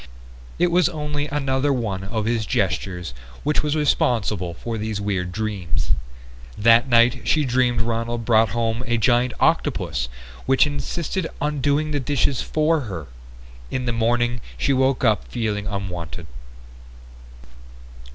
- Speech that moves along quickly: No, slow, 135 wpm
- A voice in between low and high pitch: No, low, 120 Hz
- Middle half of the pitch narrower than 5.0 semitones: No, average, 5.3 semitones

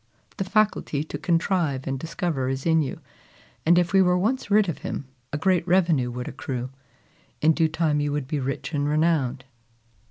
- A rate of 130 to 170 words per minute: No, average, 185 wpm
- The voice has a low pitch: No, medium, 160 Hz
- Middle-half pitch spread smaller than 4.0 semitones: No, average, 4.5 semitones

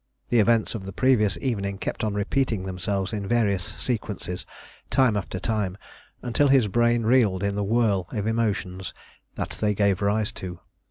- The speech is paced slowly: No, average, 165 wpm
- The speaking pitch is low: Yes, low, 105 Hz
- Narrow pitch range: No, average, 3.1 semitones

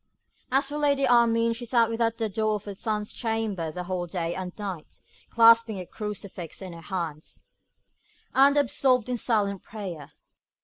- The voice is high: Yes, high, 215 Hz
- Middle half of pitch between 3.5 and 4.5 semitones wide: Yes, average, 4.1 semitones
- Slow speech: No, average, 165 wpm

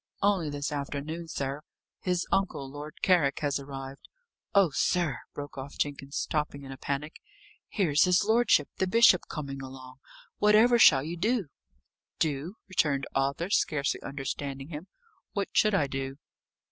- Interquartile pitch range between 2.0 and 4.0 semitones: No, average, 4.8 semitones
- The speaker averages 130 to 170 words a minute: Yes, average, 145 wpm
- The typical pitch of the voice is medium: Yes, medium, 150 Hz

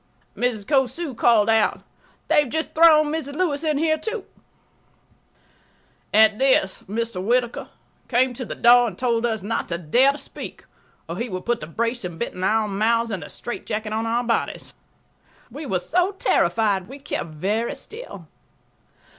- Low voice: No, high, 235 Hz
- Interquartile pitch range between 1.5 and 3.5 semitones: No, average, 4.7 semitones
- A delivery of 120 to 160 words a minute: No, average, 170 wpm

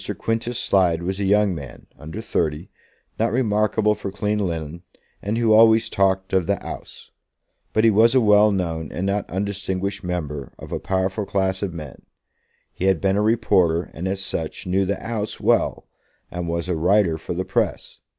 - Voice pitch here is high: No, very low, 95 Hz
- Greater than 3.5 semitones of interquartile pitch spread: No, average, 3.2 semitones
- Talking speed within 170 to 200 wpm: Yes, average, 180 wpm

